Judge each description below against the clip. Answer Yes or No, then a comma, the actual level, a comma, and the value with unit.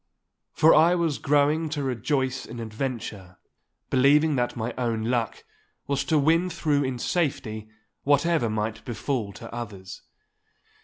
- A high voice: No, low, 130 Hz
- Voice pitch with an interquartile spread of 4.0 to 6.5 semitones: Yes, average, 4.8 semitones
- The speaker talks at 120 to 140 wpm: Yes, slow, 135 wpm